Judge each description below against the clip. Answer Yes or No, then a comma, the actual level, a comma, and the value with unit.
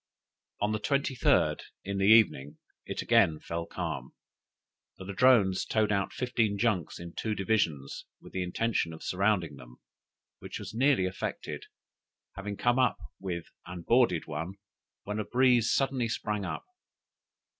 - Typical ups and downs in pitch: Yes, average, 4.6 semitones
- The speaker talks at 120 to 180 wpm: Yes, average, 145 wpm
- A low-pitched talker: Yes, low, 100 Hz